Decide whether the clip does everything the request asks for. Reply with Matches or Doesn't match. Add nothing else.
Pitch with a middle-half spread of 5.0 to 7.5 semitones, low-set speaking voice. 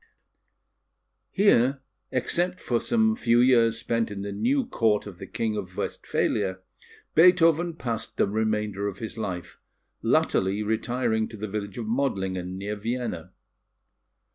Doesn't match